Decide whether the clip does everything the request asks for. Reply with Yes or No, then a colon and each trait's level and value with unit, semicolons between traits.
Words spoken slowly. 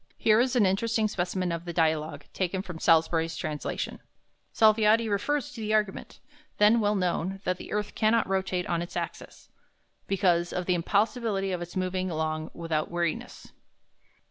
No: average, 160 wpm